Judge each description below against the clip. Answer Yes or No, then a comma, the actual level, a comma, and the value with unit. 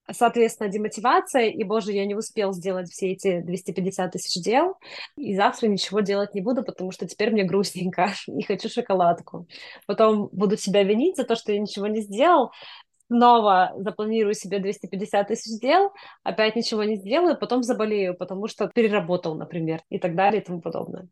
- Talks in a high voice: Yes, high, 210 Hz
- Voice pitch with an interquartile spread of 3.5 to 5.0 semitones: No, average, 2.9 semitones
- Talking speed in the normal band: No, fast, 170 wpm